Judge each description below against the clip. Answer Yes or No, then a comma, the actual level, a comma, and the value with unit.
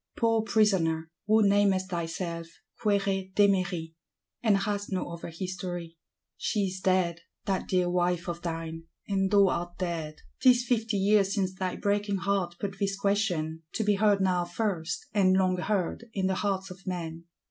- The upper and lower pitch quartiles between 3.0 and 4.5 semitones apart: No, narrow, 2.6 semitones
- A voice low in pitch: No, high, 190 Hz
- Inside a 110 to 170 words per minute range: Yes, average, 160 wpm